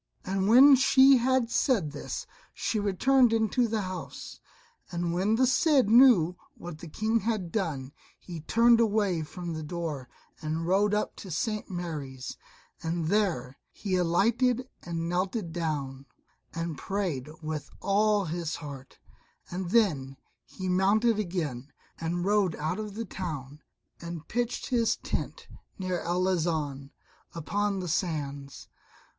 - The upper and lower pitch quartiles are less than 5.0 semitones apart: No, average, 5.3 semitones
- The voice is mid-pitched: Yes, medium, 180 Hz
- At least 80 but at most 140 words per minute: Yes, slow, 135 wpm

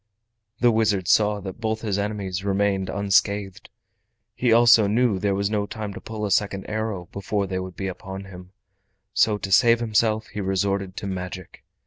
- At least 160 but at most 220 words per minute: Yes, average, 180 wpm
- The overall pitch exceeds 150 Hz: No, low, 100 Hz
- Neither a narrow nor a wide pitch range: No, narrow, 2.1 semitones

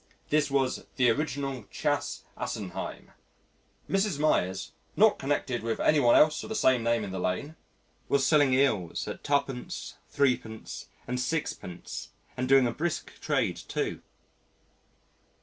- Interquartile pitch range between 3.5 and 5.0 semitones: Yes, average, 4.0 semitones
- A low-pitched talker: Yes, low, 130 Hz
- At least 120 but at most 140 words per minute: Yes, slow, 135 wpm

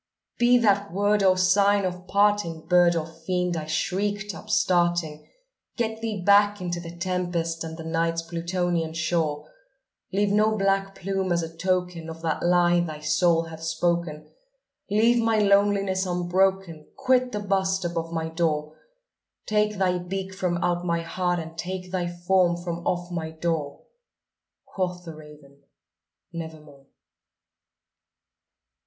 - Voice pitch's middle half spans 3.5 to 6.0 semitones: No, average, 2.9 semitones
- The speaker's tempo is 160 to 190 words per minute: No, average, 140 wpm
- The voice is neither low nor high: Yes, medium, 175 Hz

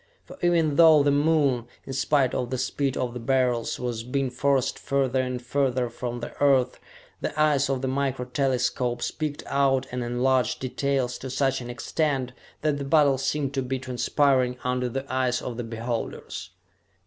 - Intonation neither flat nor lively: No, narrow, 2.0 semitones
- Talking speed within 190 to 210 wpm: No, average, 175 wpm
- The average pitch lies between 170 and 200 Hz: No, low, 130 Hz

